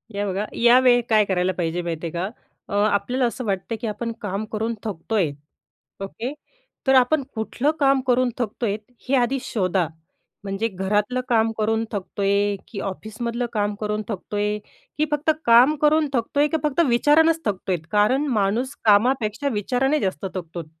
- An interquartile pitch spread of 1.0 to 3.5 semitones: No, average, 4.1 semitones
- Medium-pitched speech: No, high, 220 Hz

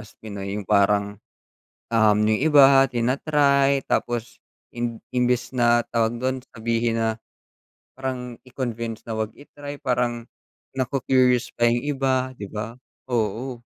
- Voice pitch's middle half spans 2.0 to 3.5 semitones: Yes, narrow, 2.5 semitones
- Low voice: Yes, low, 120 Hz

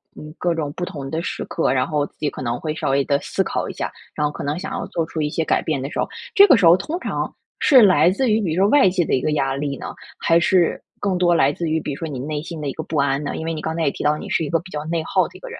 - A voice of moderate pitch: Yes, medium, 160 Hz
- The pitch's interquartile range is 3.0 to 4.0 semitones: Yes, average, 3.4 semitones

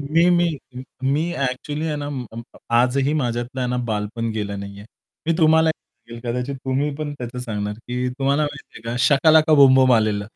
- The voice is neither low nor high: No, low, 130 Hz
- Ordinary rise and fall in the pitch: Yes, average, 4.0 semitones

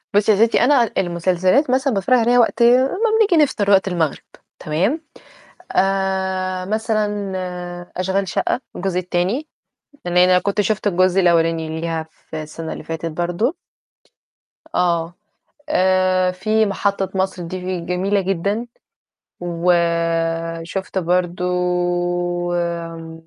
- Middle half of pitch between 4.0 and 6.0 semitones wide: No, average, 3.2 semitones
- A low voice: No, medium, 185 Hz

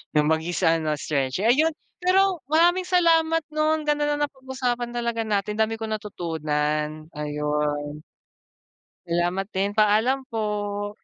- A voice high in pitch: Yes, high, 215 Hz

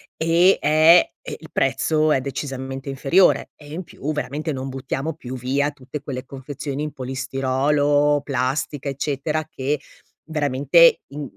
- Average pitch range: No, narrow, 2.3 semitones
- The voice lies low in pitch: No, medium, 145 Hz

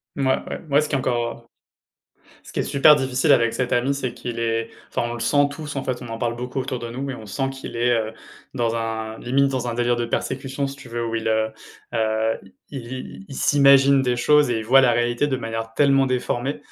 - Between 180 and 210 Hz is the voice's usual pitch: No, low, 125 Hz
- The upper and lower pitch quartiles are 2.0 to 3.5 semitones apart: Yes, average, 2.7 semitones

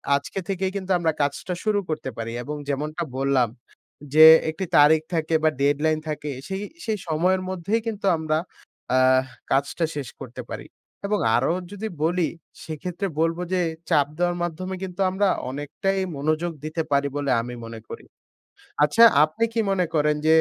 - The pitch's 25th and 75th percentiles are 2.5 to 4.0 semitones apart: No, average, 4.4 semitones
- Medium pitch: Yes, medium, 160 Hz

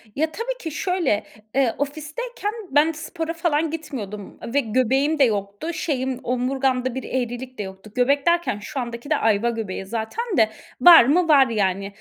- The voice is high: Yes, very high, 265 Hz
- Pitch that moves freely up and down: Yes, wide, 5.8 semitones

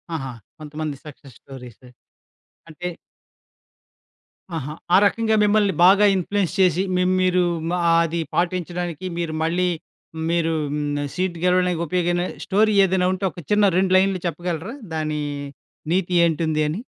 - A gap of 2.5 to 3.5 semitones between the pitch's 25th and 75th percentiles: Yes, average, 2.9 semitones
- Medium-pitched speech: Yes, medium, 175 Hz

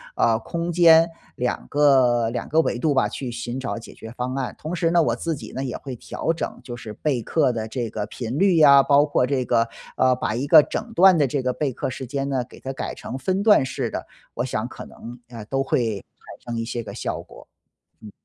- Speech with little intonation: No, average, 3.9 semitones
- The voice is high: No, low, 130 Hz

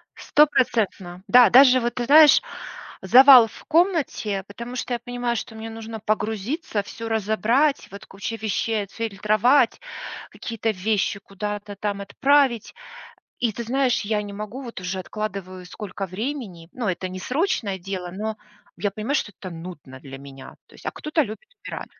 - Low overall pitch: No, high, 220 Hz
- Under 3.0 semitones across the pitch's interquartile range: No, average, 3.9 semitones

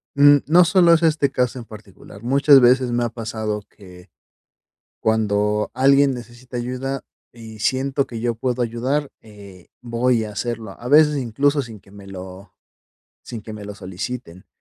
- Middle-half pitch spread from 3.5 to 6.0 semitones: Yes, average, 4.1 semitones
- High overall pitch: No, low, 120 Hz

